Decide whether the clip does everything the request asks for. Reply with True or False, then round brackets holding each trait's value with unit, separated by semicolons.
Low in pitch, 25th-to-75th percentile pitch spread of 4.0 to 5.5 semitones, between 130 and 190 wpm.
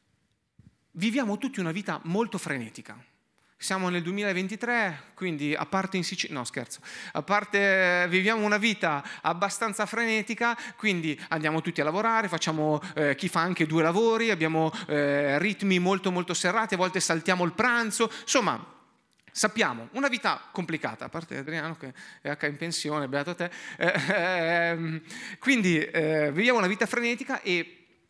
False (180 Hz; 5.0 semitones; 150 wpm)